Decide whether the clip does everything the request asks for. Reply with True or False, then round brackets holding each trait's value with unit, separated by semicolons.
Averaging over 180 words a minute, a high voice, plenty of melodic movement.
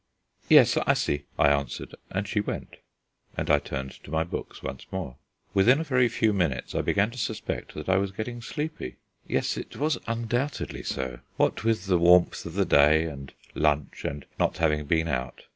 False (190 wpm; 90 Hz; 7.4 semitones)